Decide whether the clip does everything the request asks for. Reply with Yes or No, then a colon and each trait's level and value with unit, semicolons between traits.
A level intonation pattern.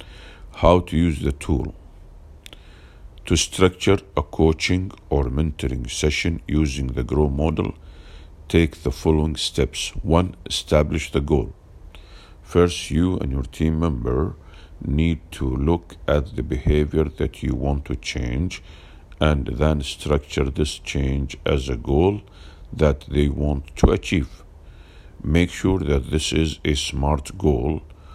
Yes: narrow, 2.2 semitones